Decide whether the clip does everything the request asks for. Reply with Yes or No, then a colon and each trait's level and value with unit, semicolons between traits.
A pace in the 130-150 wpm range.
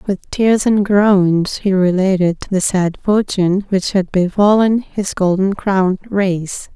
Yes: average, 140 wpm